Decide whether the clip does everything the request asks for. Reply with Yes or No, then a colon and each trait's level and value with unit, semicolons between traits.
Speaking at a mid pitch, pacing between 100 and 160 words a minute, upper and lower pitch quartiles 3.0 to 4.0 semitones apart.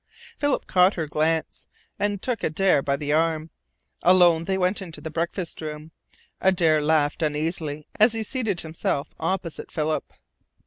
Yes: medium, 165 Hz; average, 145 wpm; average, 3.4 semitones